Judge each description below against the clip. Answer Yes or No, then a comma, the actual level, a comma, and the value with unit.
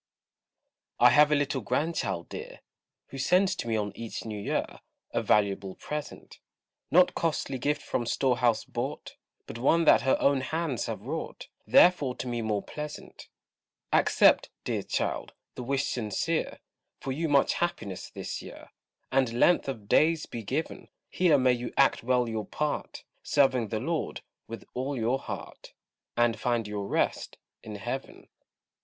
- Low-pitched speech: Yes, low, 130 Hz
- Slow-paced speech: No, average, 155 wpm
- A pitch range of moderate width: Yes, average, 4.6 semitones